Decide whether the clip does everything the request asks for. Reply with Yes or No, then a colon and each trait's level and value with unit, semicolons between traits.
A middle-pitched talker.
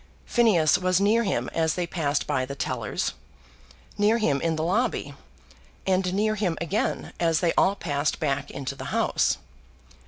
Yes: medium, 170 Hz